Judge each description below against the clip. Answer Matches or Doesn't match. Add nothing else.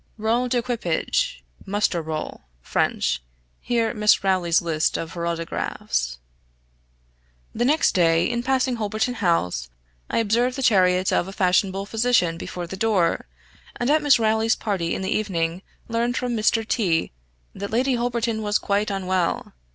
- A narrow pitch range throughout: Doesn't match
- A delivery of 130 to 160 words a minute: Matches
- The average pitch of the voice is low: Doesn't match